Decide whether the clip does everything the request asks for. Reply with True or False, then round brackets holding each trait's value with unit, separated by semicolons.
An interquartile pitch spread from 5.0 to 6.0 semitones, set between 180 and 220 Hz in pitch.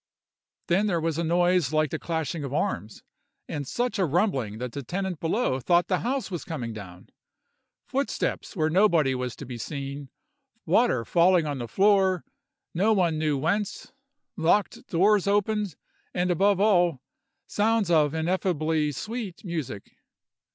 False (5.3 semitones; 170 Hz)